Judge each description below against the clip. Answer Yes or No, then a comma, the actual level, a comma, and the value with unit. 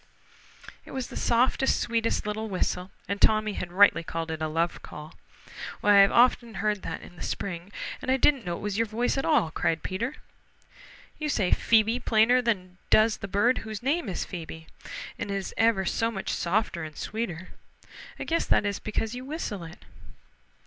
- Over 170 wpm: Yes, average, 185 wpm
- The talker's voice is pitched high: Yes, high, 210 Hz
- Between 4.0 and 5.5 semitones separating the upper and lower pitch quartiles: Yes, average, 4.3 semitones